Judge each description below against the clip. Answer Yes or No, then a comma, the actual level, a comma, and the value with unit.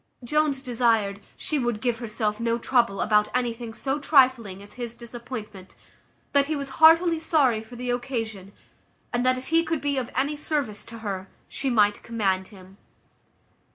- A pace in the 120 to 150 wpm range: No, average, 165 wpm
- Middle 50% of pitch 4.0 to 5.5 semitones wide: Yes, average, 4.3 semitones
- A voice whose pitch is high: Yes, high, 240 Hz